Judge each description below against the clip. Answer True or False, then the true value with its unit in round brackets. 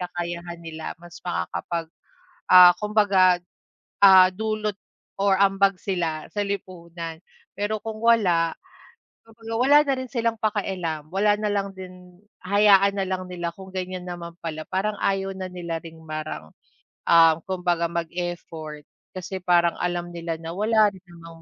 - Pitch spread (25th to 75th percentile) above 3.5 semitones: False (2.8 semitones)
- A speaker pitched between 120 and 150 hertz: False (180 Hz)